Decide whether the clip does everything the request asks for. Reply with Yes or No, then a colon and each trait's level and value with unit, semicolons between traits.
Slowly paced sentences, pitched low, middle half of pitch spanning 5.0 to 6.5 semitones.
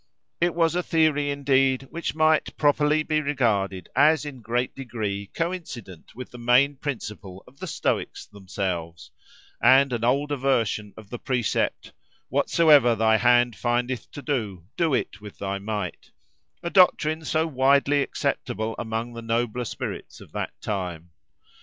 No: average, 145 wpm; low, 125 Hz; average, 5.3 semitones